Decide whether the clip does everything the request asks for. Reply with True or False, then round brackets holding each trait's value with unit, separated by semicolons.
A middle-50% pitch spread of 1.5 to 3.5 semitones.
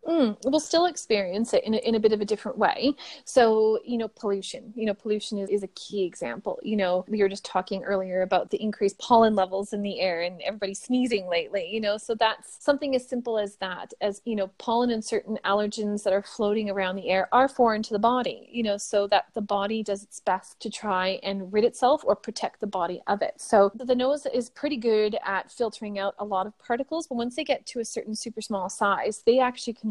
True (3.1 semitones)